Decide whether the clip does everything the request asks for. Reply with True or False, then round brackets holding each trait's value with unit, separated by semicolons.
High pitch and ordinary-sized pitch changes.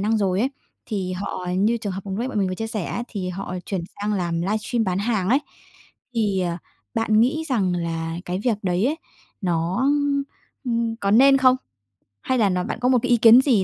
True (205 Hz; 4.3 semitones)